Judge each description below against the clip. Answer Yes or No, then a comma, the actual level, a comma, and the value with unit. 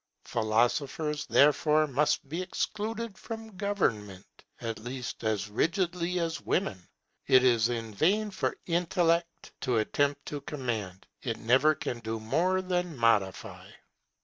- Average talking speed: No, slow, 125 wpm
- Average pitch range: No, wide, 7.5 semitones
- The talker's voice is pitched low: No, medium, 145 Hz